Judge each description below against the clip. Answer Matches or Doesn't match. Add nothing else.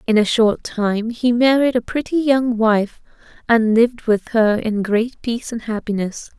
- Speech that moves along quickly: Doesn't match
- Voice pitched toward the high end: Matches